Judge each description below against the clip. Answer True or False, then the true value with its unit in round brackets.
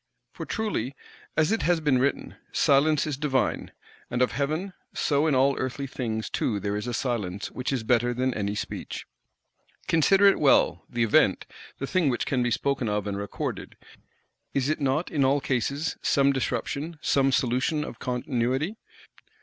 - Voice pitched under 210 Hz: True (135 Hz)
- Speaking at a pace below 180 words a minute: True (170 wpm)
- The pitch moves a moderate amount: True (3.5 semitones)